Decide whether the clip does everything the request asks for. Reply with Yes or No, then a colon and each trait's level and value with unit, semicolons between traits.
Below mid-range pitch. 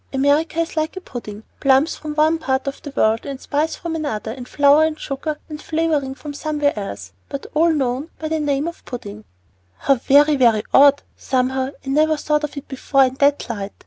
No: very high, 285 Hz